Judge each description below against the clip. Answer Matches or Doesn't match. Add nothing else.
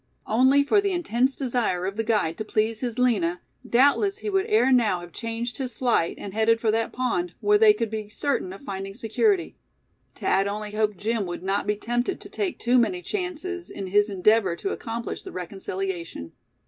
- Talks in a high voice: Matches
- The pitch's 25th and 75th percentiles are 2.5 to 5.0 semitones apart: Doesn't match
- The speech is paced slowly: Doesn't match